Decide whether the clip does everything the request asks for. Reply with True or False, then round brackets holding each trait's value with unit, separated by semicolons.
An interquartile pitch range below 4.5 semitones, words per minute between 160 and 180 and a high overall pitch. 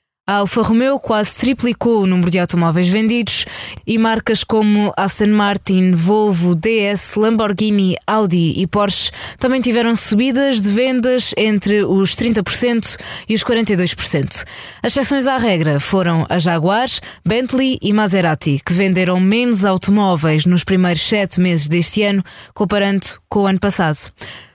False (3.6 semitones; 140 wpm; 205 Hz)